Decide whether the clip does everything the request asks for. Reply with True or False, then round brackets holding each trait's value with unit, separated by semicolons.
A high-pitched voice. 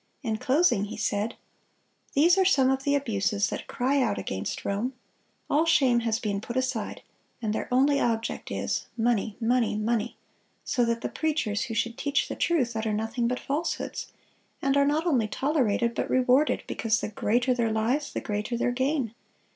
True (240 Hz)